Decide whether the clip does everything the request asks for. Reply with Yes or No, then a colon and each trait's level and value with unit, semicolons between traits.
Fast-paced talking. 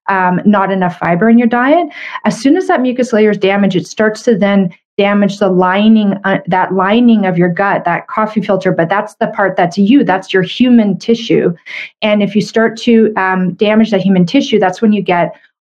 Yes: fast, 210 wpm